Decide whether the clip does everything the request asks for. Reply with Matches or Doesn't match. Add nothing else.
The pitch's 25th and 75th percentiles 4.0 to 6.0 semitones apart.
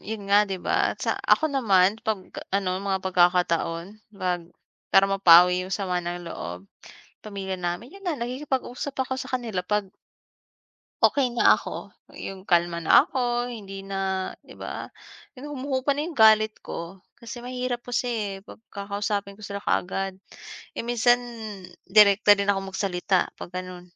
Matches